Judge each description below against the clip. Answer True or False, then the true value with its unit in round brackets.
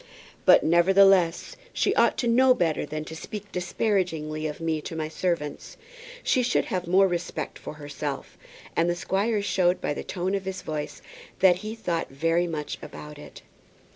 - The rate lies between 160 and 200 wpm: True (170 wpm)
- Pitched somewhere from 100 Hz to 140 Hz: False (175 Hz)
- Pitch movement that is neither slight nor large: True (3.8 semitones)